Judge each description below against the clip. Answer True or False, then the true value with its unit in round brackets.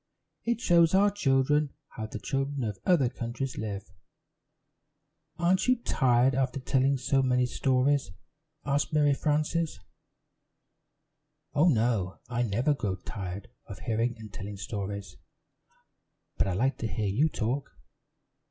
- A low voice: True (130 Hz)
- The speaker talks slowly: True (130 wpm)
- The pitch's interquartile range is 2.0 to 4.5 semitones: False (5.0 semitones)